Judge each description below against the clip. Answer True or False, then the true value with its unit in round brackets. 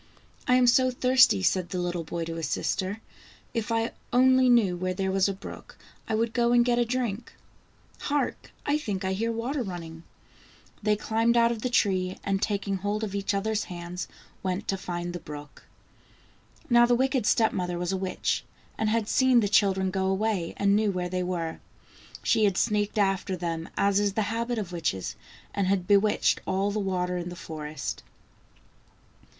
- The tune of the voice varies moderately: True (4.0 semitones)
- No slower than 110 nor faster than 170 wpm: False (190 wpm)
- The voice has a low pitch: False (200 Hz)